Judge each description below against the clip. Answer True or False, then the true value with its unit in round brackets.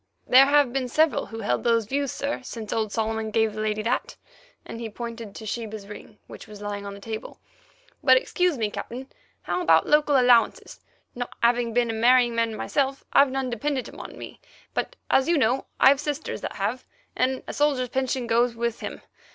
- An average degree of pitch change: True (3.3 semitones)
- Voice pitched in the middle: False (240 Hz)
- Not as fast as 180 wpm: False (190 wpm)